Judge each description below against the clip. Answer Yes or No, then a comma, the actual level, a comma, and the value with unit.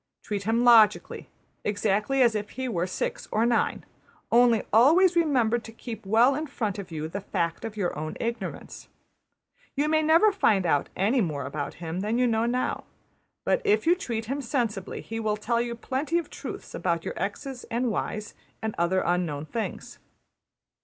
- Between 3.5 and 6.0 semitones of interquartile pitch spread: Yes, average, 4.5 semitones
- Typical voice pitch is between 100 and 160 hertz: No, high, 225 Hz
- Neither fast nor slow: Yes, average, 180 wpm